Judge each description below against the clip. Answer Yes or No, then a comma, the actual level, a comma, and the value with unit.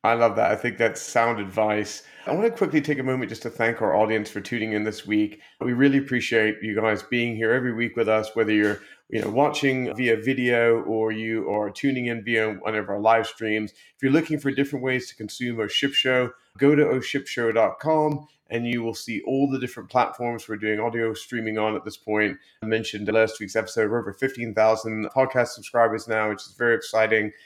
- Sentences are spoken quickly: Yes, fast, 220 wpm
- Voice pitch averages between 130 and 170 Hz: No, low, 115 Hz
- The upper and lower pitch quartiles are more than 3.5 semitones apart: No, average, 2.7 semitones